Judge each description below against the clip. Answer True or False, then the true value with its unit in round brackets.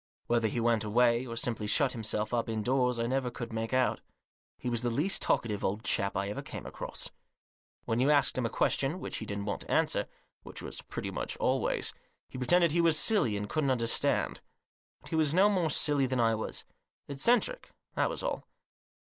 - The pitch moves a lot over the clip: False (4.3 semitones)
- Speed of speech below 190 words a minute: False (200 wpm)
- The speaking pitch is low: True (125 Hz)